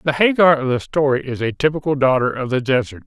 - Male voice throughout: Yes, male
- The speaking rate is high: Yes, fast, 235 wpm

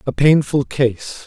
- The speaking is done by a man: Yes, male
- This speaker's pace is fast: No, average, 140 wpm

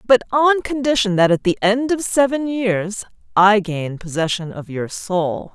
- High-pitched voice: Yes, high, 215 Hz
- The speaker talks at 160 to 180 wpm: Yes, average, 175 wpm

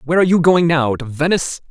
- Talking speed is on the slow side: No, fast, 210 wpm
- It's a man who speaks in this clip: Yes, male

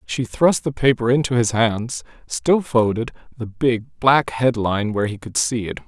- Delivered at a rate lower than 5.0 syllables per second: Yes, 4.7 syllables/s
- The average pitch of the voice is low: Yes, low, 120 Hz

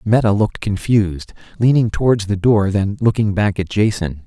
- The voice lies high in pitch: No, low, 105 Hz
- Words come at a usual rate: Yes, average, 170 wpm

